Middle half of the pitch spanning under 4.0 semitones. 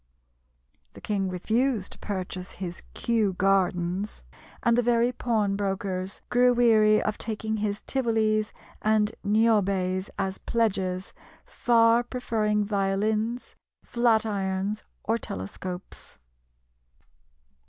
Yes: average, 2.9 semitones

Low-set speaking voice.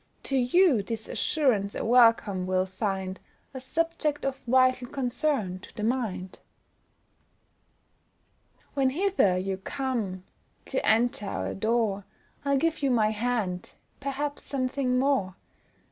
No: high, 245 Hz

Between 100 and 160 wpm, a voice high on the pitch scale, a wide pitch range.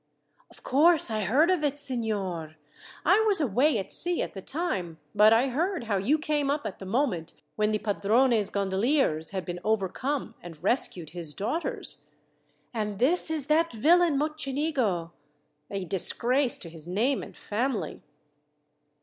Yes: average, 155 wpm; high, 230 Hz; wide, 7.2 semitones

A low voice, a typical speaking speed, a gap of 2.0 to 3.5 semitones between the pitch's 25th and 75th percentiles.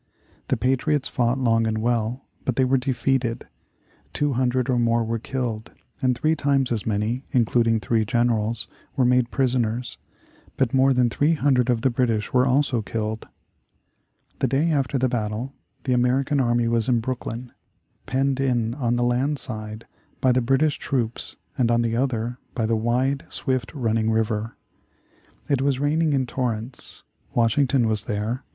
Yes: low, 125 Hz; average, 160 wpm; narrow, 2.5 semitones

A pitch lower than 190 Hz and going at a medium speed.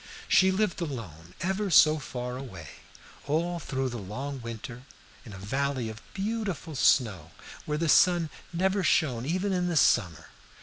Yes: medium, 140 Hz; average, 155 wpm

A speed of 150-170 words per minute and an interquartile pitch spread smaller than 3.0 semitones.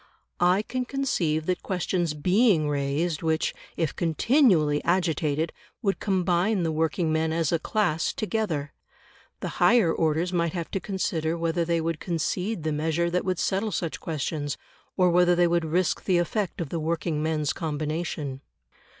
Yes: average, 160 wpm; narrow, 2.6 semitones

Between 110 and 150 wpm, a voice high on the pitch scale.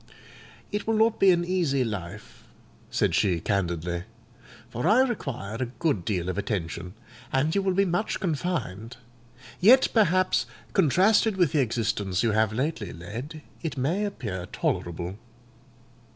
No: average, 140 wpm; low, 130 Hz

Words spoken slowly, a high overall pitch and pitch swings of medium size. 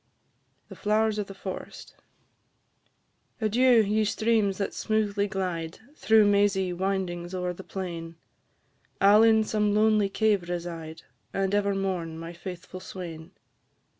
Yes: slow, 130 wpm; high, 195 Hz; average, 3.1 semitones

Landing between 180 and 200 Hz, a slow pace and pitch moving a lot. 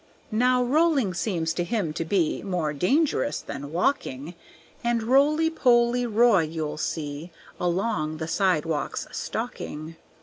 Yes: medium, 185 Hz; slow, 125 wpm; wide, 7.3 semitones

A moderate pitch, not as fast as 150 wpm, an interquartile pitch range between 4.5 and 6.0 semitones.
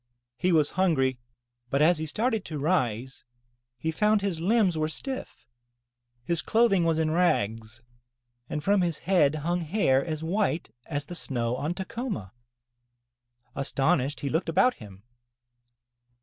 Yes: medium, 160 Hz; average, 140 wpm; average, 5.2 semitones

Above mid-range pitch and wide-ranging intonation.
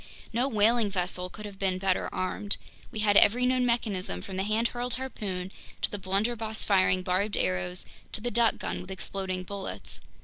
No: high, 200 Hz; average, 3.6 semitones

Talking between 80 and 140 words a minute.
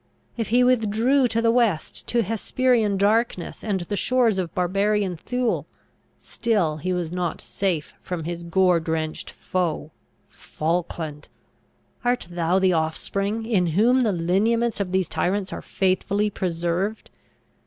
Yes: slow, 135 wpm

